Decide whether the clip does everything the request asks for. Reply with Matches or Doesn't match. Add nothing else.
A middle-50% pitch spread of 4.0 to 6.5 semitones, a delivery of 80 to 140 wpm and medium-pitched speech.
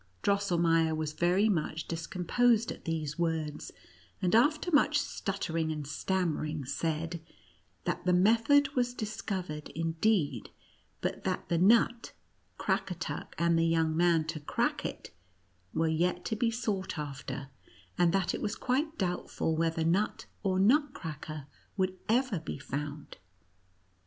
Matches